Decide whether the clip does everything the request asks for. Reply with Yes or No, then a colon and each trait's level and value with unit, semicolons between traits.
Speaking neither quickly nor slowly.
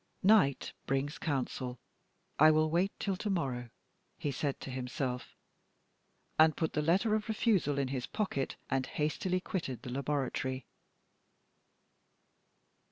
No: slow, 125 wpm